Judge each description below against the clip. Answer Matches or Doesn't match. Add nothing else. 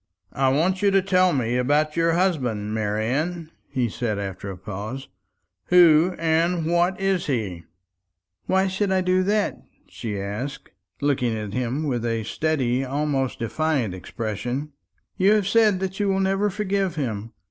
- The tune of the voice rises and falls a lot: Matches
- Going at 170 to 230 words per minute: Doesn't match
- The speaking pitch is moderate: Matches